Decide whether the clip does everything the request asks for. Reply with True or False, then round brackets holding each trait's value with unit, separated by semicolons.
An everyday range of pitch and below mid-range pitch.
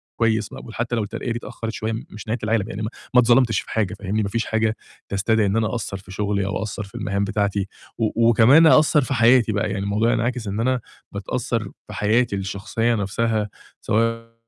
False (2.3 semitones; 110 Hz)